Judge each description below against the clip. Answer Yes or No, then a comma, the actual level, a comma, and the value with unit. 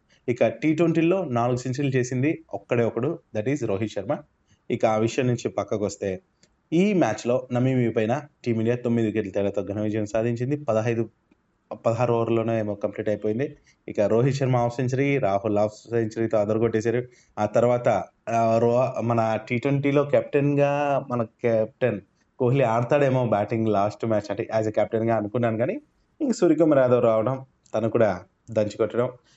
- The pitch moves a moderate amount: Yes, average, 3.1 semitones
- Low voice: Yes, low, 120 Hz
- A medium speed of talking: No, fast, 145 wpm